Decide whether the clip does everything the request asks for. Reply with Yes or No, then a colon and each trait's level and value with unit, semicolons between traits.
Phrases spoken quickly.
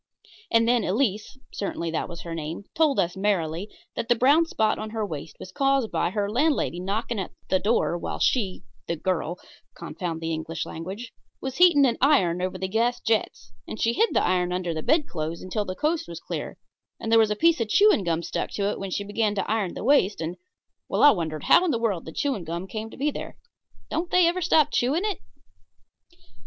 Yes: fast, 215 wpm